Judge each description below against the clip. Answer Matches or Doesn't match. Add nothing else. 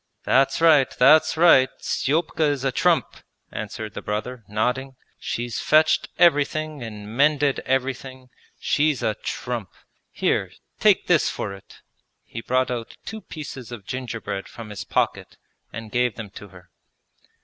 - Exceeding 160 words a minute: Doesn't match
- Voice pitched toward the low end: Matches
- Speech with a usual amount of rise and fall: Matches